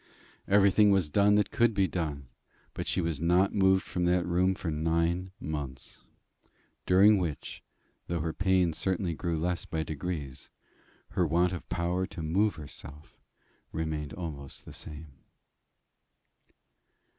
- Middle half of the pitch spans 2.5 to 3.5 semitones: Yes, average, 3.1 semitones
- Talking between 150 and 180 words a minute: No, slow, 135 wpm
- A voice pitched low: Yes, very low, 85 Hz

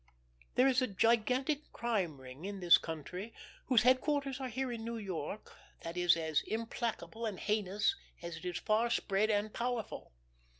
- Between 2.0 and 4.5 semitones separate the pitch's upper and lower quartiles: No, average, 5.2 semitones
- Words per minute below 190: Yes, average, 165 wpm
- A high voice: Yes, high, 215 Hz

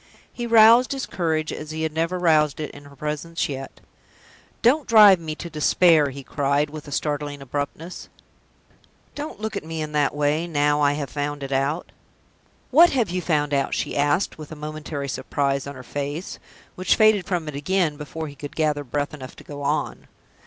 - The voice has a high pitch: No, medium, 150 Hz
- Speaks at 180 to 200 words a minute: Yes, average, 195 wpm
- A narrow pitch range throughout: No, average, 3.0 semitones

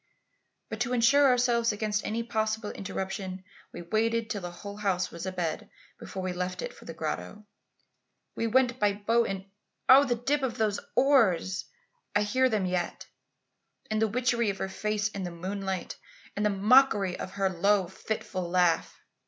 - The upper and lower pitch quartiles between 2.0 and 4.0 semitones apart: Yes, average, 3.6 semitones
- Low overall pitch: No, high, 210 Hz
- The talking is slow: No, average, 170 wpm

